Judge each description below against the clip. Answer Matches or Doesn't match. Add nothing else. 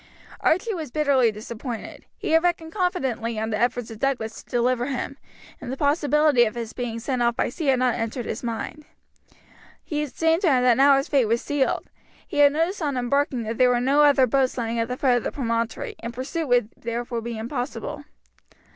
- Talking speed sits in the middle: Doesn't match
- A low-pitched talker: Doesn't match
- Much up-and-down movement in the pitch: Doesn't match